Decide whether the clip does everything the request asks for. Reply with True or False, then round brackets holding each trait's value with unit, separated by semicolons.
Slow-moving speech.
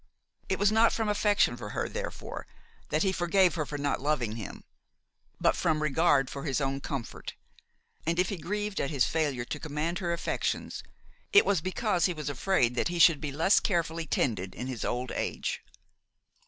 False (185 wpm)